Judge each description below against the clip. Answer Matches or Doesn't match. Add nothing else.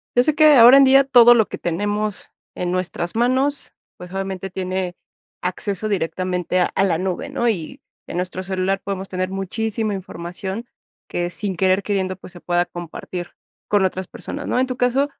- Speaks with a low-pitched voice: Doesn't match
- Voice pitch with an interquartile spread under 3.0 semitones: Doesn't match